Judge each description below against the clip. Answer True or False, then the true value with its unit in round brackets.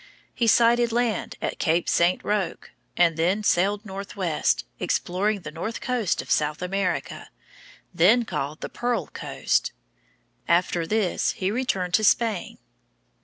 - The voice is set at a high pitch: True (195 Hz)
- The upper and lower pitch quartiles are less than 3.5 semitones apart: False (4.2 semitones)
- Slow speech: True (130 wpm)